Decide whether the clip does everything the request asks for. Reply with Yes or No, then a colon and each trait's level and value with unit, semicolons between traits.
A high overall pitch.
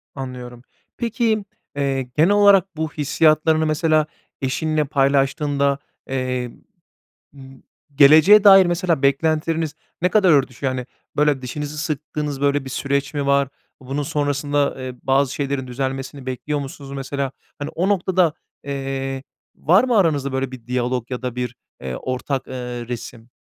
No: medium, 140 Hz